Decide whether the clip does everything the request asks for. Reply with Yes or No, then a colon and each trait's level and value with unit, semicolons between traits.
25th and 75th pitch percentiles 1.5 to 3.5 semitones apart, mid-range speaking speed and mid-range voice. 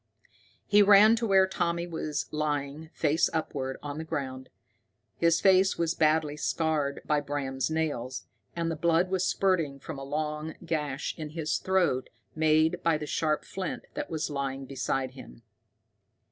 Yes: average, 3.0 semitones; average, 155 wpm; medium, 155 Hz